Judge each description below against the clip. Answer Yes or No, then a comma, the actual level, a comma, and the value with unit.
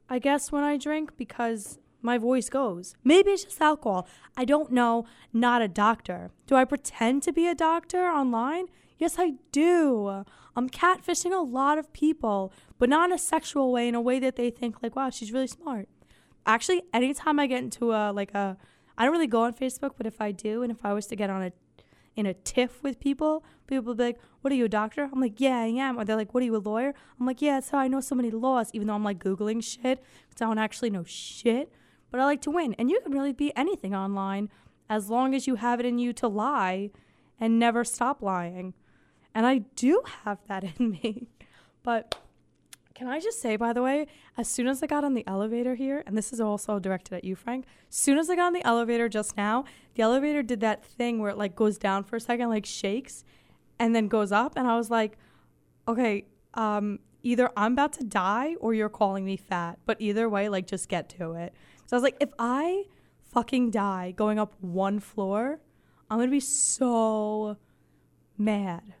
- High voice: Yes, high, 240 Hz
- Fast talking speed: Yes, fast, 225 wpm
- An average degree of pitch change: Yes, average, 4.3 semitones